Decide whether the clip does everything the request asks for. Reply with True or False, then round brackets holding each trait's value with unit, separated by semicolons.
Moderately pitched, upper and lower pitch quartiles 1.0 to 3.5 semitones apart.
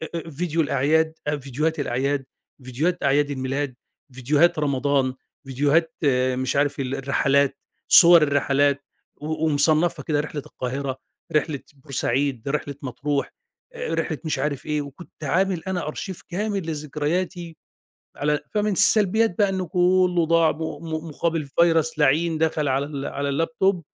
True (150 Hz; 3.2 semitones)